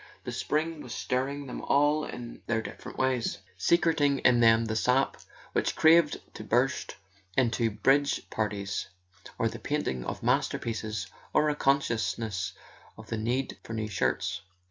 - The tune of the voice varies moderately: Yes, average, 4.3 semitones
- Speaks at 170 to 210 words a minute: No, average, 145 wpm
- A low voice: Yes, low, 120 Hz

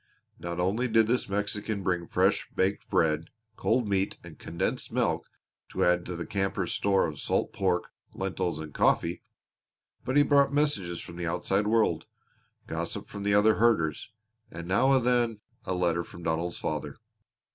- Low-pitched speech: Yes, very low, 95 Hz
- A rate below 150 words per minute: No, average, 165 wpm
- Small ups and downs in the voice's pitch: No, average, 4.3 semitones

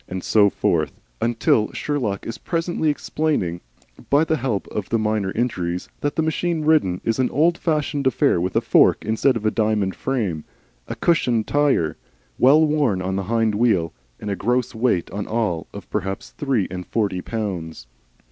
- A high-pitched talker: No, low, 110 Hz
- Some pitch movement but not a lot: No, wide, 6.7 semitones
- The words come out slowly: No, average, 175 wpm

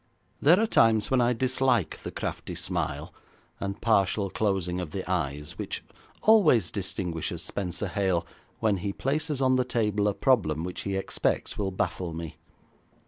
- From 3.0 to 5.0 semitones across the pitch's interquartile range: No, wide, 5.4 semitones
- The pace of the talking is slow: No, average, 155 wpm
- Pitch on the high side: No, low, 100 Hz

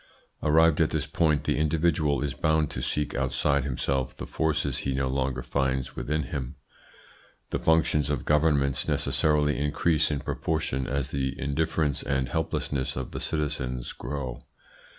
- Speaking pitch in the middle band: No, very low, 70 Hz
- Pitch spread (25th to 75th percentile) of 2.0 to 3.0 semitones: Yes, narrow, 2.4 semitones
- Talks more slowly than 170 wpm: Yes, average, 150 wpm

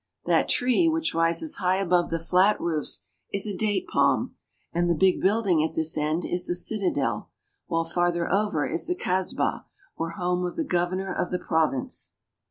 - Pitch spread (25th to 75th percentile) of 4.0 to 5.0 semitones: No, average, 2.9 semitones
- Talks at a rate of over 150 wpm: Yes, average, 180 wpm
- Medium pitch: Yes, medium, 180 Hz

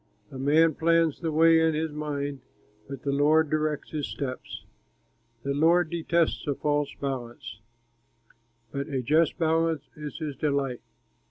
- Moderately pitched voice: Yes, medium, 150 Hz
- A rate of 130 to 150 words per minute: Yes, average, 145 wpm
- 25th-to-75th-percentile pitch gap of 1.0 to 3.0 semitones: Yes, narrow, 2.5 semitones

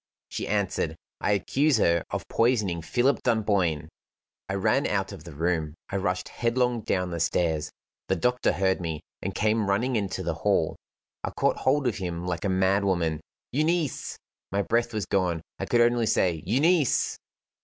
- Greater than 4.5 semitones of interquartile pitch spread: Yes, wide, 5.5 semitones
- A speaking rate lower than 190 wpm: Yes, average, 165 wpm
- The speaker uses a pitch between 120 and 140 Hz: No, low, 100 Hz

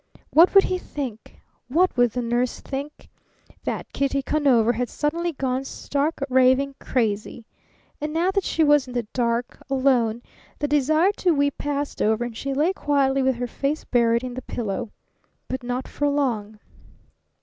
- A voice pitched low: No, very high, 270 Hz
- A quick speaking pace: No, average, 165 wpm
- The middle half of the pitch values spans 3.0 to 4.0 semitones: Yes, average, 3.3 semitones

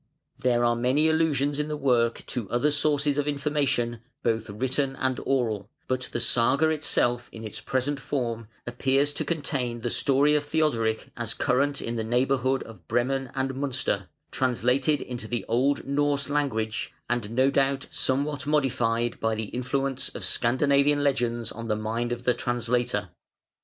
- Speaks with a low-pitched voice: Yes, low, 130 Hz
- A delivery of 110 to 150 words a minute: No, average, 160 wpm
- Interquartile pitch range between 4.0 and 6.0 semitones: No, average, 3.1 semitones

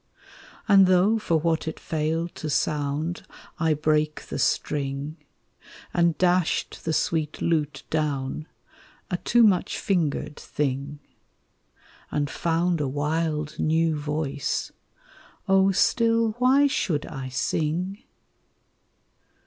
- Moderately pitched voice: Yes, medium, 160 Hz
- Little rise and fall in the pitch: No, average, 3.2 semitones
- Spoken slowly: Yes, slow, 110 wpm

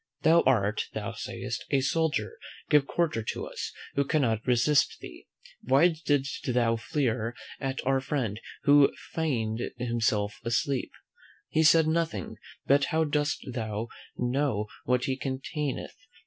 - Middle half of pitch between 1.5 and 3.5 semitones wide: No, average, 4.2 semitones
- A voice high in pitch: No, low, 135 Hz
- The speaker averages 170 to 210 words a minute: No, slow, 135 wpm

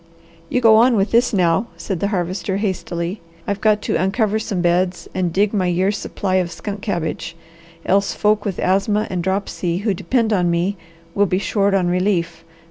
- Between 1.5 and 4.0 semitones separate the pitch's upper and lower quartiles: Yes, average, 2.8 semitones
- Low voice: No, high, 195 Hz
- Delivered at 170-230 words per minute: Yes, average, 185 wpm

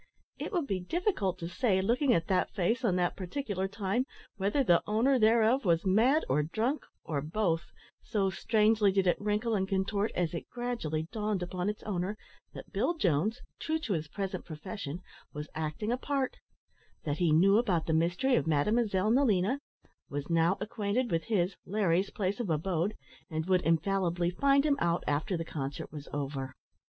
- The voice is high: Yes, high, 195 Hz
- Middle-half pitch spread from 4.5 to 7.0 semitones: Yes, average, 5.0 semitones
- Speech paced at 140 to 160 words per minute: No, average, 175 wpm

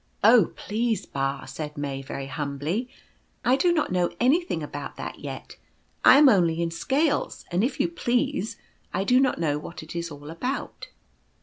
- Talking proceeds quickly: No, average, 175 wpm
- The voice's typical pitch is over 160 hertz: Yes, medium, 185 Hz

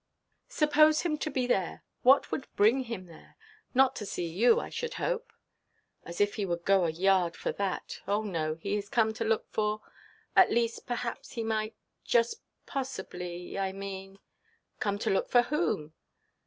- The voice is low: No, high, 215 Hz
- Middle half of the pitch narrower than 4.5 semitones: No, average, 4.8 semitones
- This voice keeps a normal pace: Yes, average, 170 wpm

